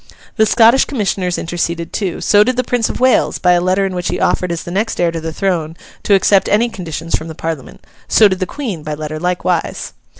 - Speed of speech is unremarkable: No, fast, 230 wpm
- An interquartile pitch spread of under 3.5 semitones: No, average, 3.9 semitones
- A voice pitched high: No, medium, 180 Hz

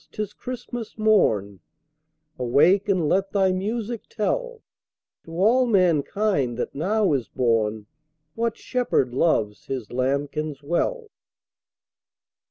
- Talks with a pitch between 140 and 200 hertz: Yes, medium, 185 Hz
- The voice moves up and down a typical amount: No, wide, 8.5 semitones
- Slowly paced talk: Yes, slow, 110 wpm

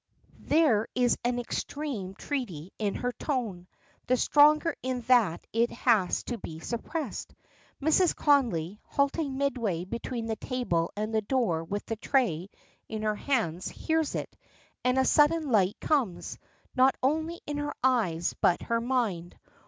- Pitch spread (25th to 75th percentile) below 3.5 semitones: No, wide, 5.6 semitones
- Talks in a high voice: Yes, high, 240 Hz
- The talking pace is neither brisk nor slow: Yes, average, 145 wpm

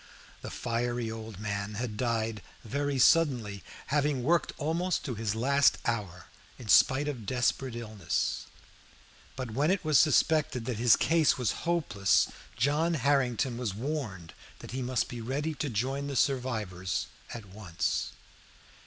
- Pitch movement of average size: Yes, average, 4.5 semitones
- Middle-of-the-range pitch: No, low, 125 Hz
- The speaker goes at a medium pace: Yes, average, 145 wpm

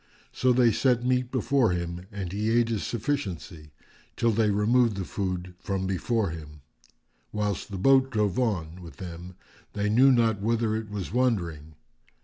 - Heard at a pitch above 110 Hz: No, low, 105 Hz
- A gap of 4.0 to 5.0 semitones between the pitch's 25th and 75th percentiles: Yes, average, 4.6 semitones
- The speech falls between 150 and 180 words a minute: Yes, average, 160 wpm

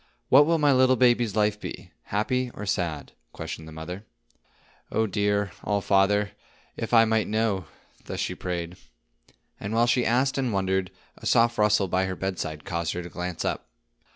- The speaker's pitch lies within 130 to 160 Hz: No, low, 105 Hz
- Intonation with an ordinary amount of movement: Yes, average, 4.1 semitones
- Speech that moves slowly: No, average, 170 wpm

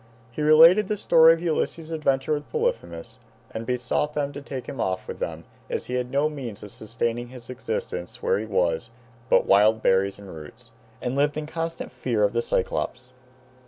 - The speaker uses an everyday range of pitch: No, wide, 5.9 semitones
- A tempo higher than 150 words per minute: Yes, average, 190 wpm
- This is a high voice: No, low, 125 Hz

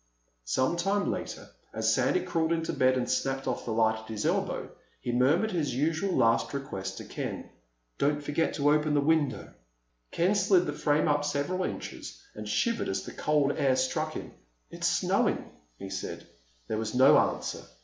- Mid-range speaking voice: Yes, medium, 145 Hz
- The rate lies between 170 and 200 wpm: Yes, average, 180 wpm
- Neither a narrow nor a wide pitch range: Yes, average, 4.4 semitones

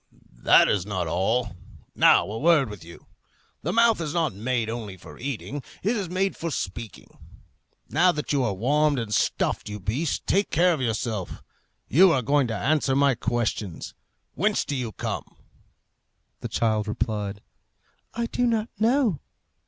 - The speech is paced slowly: No, average, 160 wpm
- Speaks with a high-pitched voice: No, low, 130 Hz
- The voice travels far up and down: Yes, wide, 7.8 semitones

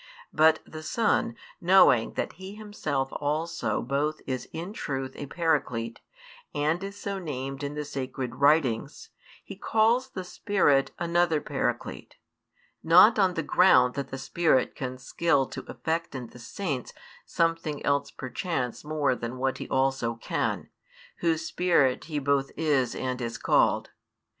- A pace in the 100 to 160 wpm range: Yes, average, 145 wpm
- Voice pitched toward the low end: No, medium, 150 Hz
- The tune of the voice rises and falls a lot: No, average, 4.4 semitones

